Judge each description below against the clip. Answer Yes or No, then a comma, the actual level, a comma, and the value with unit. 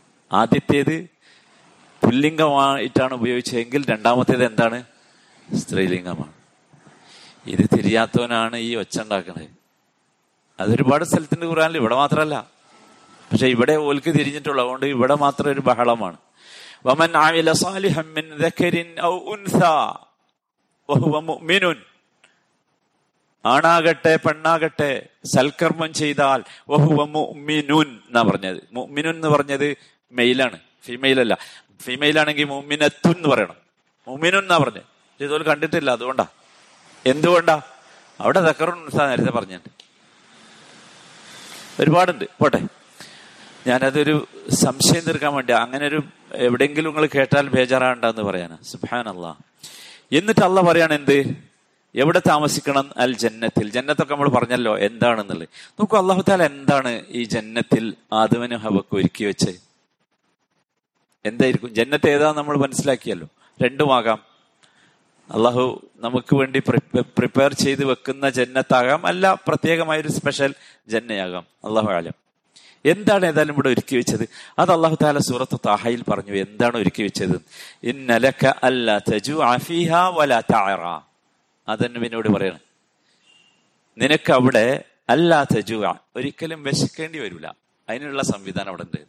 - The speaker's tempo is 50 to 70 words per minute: No, average, 90 wpm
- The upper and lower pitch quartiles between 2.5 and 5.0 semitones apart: Yes, average, 4.1 semitones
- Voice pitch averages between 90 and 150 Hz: Yes, medium, 140 Hz